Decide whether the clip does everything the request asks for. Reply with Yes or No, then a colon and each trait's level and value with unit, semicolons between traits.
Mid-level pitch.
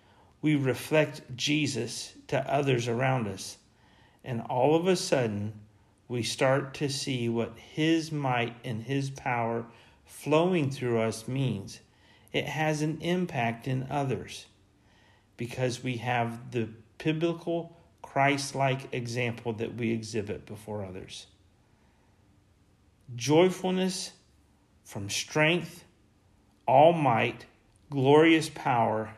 No: low, 120 Hz